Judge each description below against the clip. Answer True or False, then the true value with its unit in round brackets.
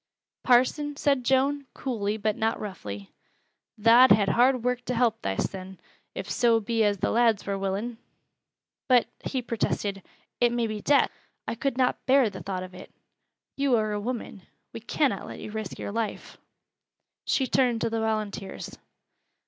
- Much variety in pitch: False (3.5 semitones)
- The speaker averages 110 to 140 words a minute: False (165 wpm)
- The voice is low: False (225 Hz)